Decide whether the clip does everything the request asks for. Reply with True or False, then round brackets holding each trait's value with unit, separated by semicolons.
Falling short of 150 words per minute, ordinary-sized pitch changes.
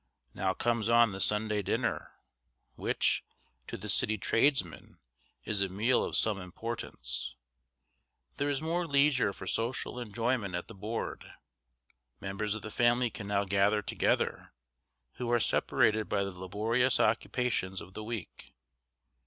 True (140 wpm; 3.4 semitones)